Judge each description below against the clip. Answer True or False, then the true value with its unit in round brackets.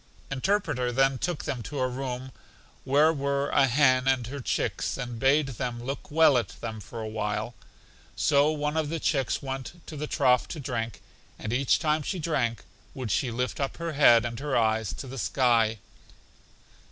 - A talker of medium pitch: False (130 Hz)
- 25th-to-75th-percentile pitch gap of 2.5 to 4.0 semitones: True (3.4 semitones)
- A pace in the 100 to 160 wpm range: False (185 wpm)